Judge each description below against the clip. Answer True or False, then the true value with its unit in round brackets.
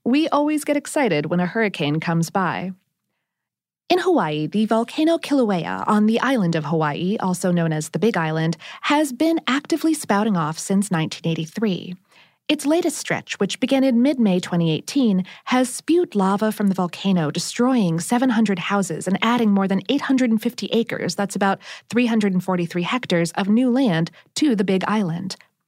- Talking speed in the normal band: True (155 wpm)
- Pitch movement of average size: False (6.2 semitones)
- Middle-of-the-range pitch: False (205 Hz)